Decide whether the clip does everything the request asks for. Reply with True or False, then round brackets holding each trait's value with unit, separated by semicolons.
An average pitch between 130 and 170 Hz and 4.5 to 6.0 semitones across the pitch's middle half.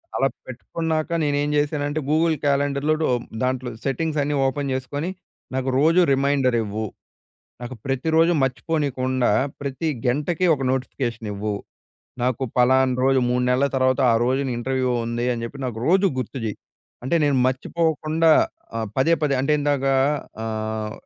False (135 Hz; 2.8 semitones)